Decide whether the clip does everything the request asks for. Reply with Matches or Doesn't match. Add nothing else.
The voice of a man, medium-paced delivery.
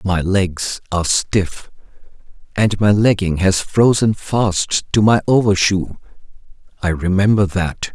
Doesn't match